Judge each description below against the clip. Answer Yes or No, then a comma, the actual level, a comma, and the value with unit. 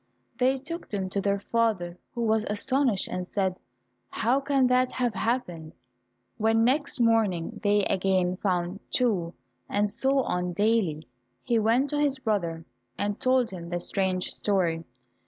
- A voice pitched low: No, high, 210 Hz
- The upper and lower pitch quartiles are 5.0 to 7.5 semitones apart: Yes, average, 5.3 semitones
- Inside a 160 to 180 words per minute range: No, average, 150 wpm